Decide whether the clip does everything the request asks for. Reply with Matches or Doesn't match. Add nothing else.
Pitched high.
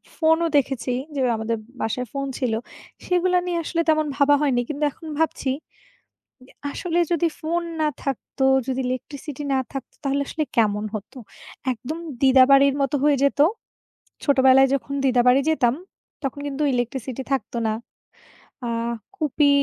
Matches